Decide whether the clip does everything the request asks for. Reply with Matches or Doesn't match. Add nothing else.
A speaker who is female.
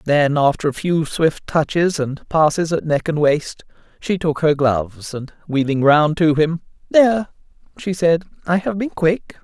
Doesn't match